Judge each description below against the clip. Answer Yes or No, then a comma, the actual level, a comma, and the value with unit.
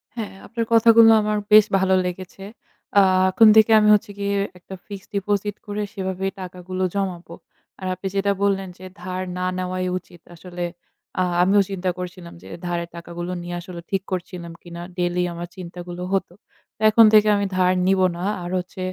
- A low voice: No, medium, 185 Hz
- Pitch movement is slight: Yes, narrow, 2.2 semitones